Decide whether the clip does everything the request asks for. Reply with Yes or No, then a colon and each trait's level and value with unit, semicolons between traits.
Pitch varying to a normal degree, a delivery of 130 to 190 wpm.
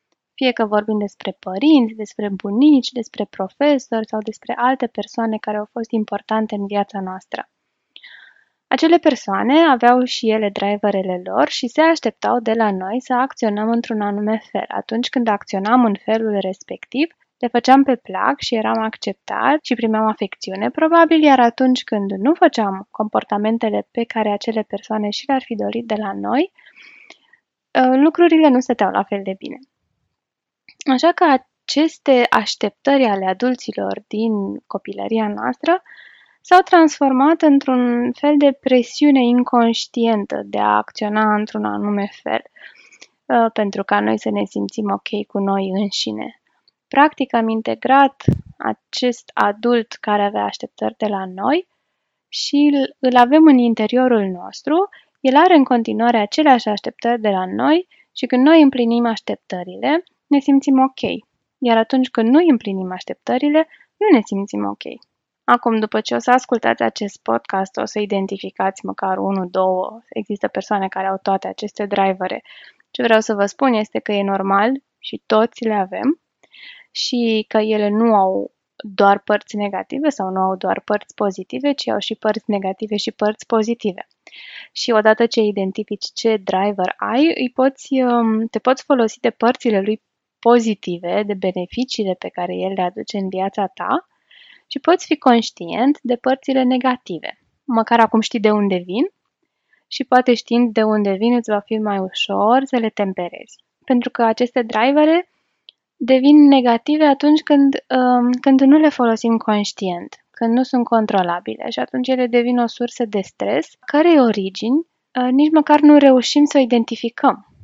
Yes: average, 4.4 semitones; average, 155 wpm